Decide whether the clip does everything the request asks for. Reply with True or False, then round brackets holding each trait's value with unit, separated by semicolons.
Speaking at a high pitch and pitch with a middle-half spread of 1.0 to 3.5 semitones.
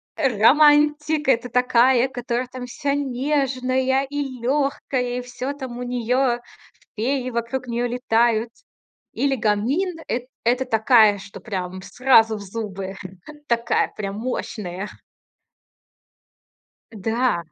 True (250 Hz; 2.9 semitones)